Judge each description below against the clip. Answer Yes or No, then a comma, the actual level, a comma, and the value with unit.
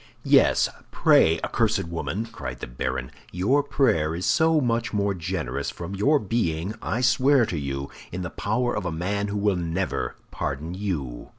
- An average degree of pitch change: No, wide, 6.0 semitones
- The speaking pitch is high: No, very low, 95 Hz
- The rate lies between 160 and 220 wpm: Yes, average, 175 wpm